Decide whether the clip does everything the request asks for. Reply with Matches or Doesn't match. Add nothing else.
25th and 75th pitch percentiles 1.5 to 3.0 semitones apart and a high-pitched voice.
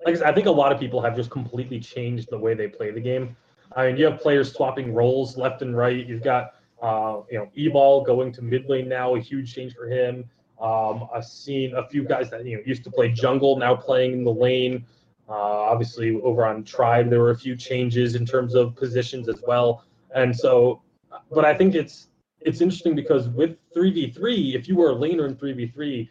Doesn't match